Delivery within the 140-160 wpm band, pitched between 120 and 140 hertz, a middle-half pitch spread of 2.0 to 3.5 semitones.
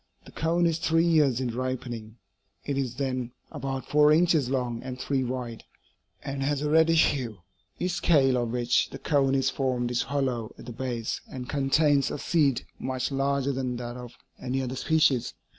No: average, 180 wpm; low, 135 Hz; average, 2.8 semitones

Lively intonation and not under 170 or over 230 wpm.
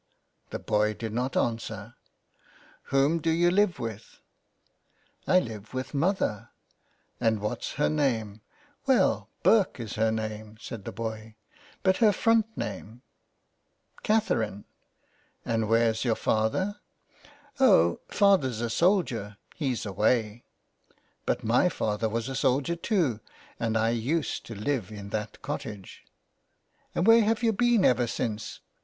No: wide, 8.8 semitones; average, 160 wpm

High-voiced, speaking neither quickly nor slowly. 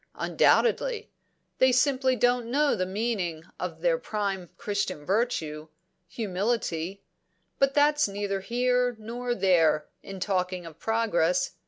No: high, 210 Hz; slow, 120 wpm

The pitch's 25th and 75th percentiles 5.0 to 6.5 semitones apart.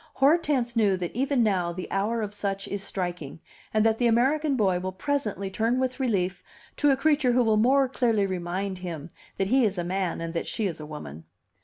Yes: wide, 5.5 semitones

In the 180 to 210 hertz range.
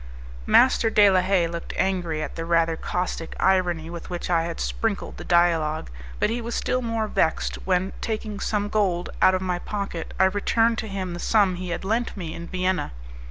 Yes: medium, 185 Hz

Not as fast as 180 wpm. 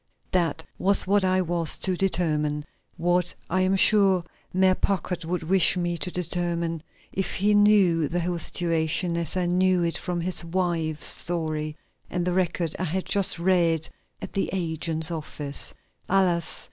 Yes: average, 160 wpm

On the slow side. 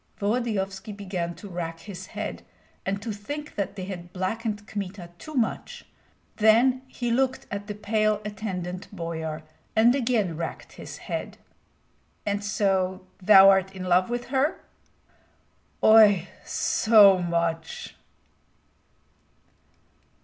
Yes: slow, 120 wpm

